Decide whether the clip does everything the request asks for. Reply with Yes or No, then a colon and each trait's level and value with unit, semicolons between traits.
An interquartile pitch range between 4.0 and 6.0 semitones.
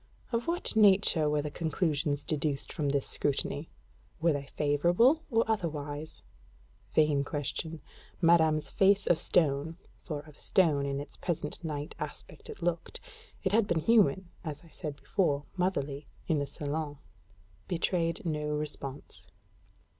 No: average, 3.3 semitones